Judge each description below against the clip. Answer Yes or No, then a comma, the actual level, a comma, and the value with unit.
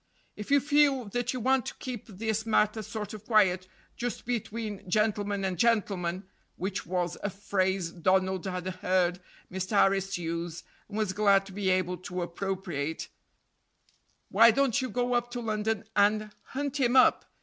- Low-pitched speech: No, high, 205 Hz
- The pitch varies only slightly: No, average, 3.6 semitones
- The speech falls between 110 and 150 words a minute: No, average, 160 wpm